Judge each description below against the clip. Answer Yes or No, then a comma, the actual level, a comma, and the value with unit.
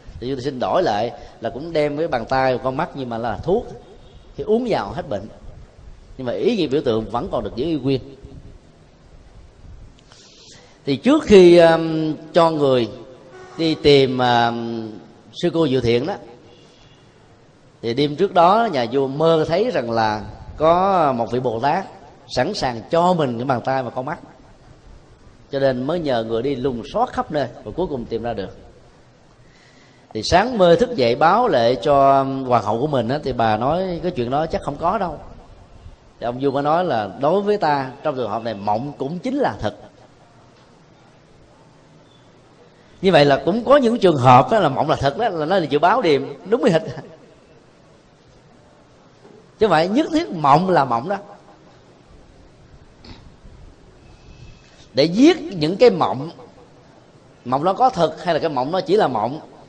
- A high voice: No, low, 135 Hz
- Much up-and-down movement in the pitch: Yes, wide, 5.8 semitones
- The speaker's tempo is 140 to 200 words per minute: Yes, average, 180 wpm